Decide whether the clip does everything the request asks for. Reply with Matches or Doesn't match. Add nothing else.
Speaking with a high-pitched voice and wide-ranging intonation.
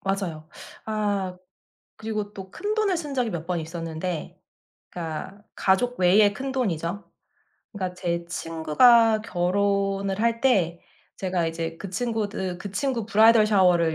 Doesn't match